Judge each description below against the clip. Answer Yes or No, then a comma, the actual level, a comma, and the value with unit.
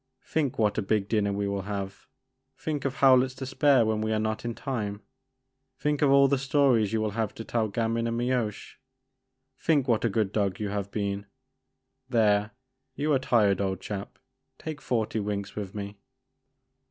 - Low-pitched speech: Yes, low, 110 Hz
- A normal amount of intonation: Yes, average, 4.3 semitones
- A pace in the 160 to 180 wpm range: No, average, 195 wpm